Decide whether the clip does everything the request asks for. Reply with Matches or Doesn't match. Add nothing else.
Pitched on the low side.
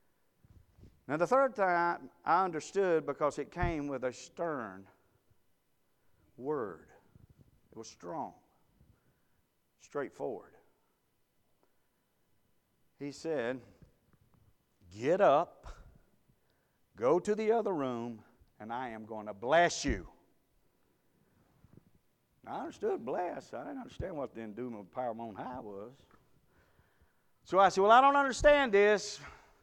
Doesn't match